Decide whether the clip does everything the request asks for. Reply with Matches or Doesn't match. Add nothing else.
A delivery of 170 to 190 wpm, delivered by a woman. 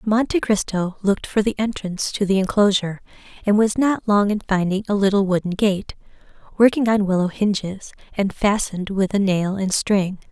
Matches